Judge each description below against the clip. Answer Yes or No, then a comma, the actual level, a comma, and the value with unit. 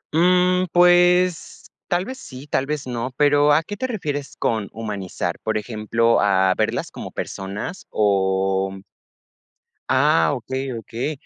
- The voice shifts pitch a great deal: Yes, wide, 8.5 semitones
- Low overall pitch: Yes, low, 130 Hz